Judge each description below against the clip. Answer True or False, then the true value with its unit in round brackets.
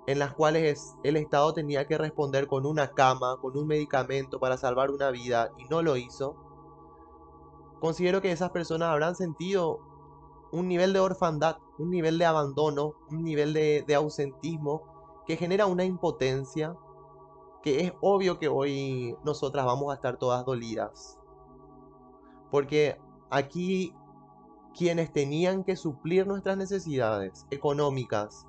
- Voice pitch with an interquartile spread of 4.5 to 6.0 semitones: False (3.2 semitones)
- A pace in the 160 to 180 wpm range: False (135 wpm)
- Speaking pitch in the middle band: True (150 Hz)